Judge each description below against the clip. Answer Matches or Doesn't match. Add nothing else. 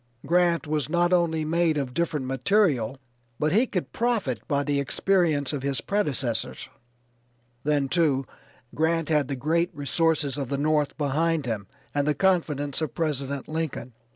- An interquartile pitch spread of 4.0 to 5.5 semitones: Doesn't match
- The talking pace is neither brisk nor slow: Matches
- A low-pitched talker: Doesn't match